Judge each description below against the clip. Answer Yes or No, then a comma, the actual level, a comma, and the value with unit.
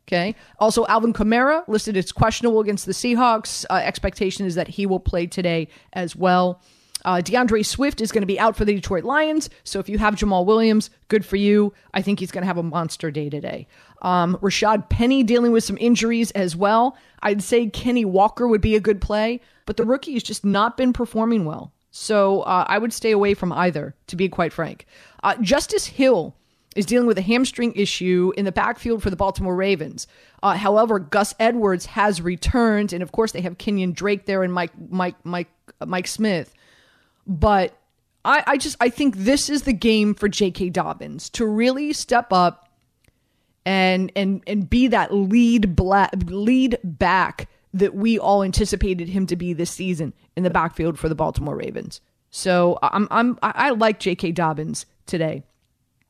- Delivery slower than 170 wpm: No, average, 190 wpm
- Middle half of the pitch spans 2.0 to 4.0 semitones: Yes, average, 3.7 semitones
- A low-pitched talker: No, high, 200 Hz